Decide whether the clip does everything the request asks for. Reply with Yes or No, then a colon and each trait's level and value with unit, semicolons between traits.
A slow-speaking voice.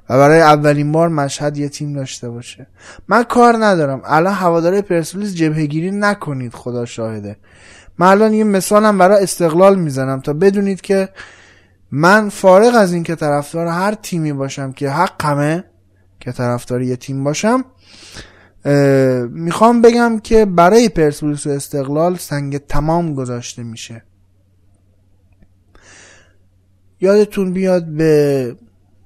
No: average, 125 wpm